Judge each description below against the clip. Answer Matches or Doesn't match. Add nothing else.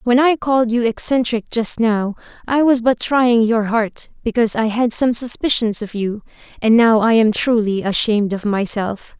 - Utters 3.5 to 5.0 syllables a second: Matches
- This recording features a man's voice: Doesn't match